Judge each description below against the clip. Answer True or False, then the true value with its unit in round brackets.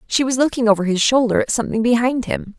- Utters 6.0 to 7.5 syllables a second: True (6.5 syllables/s)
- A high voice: True (235 Hz)